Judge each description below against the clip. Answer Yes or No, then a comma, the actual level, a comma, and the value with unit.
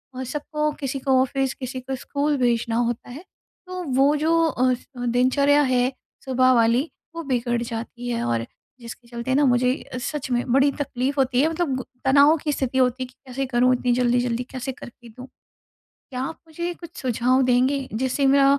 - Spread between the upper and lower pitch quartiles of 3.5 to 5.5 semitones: No, narrow, 2.4 semitones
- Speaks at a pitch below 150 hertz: No, very high, 260 Hz